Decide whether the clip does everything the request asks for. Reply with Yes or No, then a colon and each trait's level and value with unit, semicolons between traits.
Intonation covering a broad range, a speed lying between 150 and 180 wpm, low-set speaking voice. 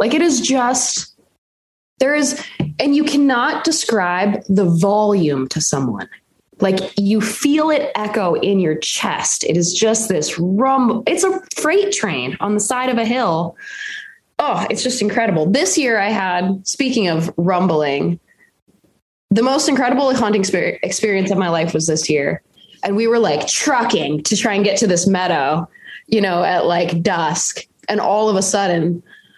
No: wide, 6.2 semitones; average, 165 wpm; high, 210 Hz